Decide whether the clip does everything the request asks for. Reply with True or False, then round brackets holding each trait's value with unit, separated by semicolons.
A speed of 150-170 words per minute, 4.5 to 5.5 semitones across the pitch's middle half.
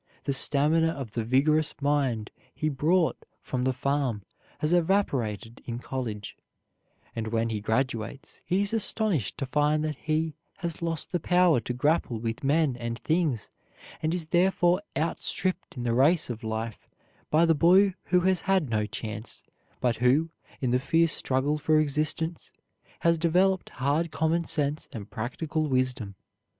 True (160 wpm; 5.2 semitones)